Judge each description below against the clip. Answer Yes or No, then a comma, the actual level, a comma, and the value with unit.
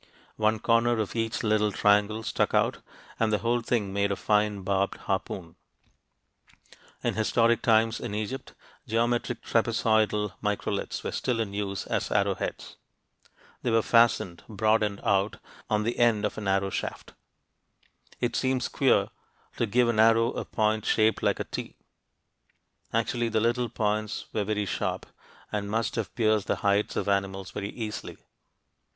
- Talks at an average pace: Yes, average, 155 wpm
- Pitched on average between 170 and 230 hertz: No, low, 110 Hz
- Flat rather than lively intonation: Yes, narrow, 2.0 semitones